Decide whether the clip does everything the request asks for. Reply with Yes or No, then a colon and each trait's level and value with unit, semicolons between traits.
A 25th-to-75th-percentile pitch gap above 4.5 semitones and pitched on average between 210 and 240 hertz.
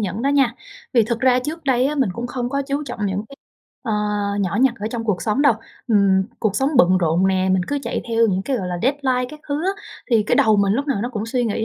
Yes: average, 5.1 semitones; high, 235 Hz